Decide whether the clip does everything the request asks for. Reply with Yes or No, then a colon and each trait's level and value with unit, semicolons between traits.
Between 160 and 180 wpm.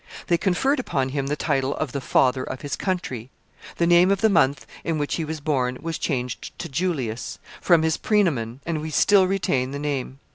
No: fast, 205 wpm